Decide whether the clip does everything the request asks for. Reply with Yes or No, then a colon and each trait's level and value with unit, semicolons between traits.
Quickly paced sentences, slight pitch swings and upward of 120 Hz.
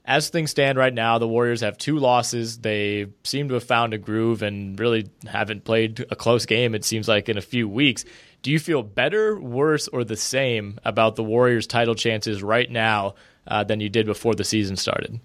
No: fast, 210 wpm; narrow, 2.3 semitones; low, 115 Hz